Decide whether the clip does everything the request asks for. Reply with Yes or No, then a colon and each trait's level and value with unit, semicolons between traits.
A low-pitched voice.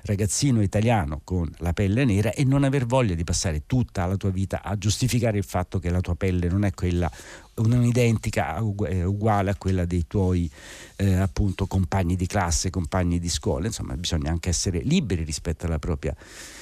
Yes: very low, 95 Hz